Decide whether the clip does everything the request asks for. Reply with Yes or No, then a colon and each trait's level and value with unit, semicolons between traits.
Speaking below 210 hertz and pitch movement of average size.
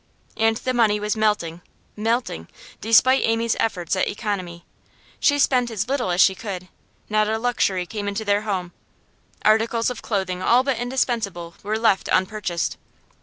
No: high, 215 Hz; average, 3.6 semitones